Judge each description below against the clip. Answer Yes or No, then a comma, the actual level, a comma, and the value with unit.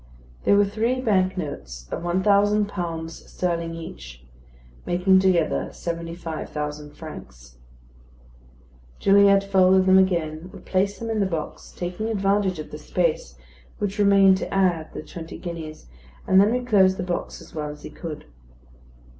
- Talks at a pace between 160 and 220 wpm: No, average, 150 wpm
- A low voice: No, medium, 185 Hz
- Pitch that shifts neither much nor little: Yes, average, 3.5 semitones